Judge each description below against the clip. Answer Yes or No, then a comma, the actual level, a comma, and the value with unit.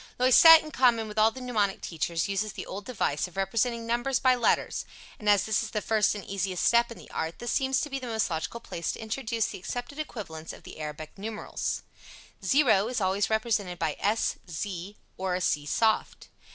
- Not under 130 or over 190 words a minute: No, fast, 205 wpm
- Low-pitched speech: No, high, 215 Hz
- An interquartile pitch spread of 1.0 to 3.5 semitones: No, average, 4.2 semitones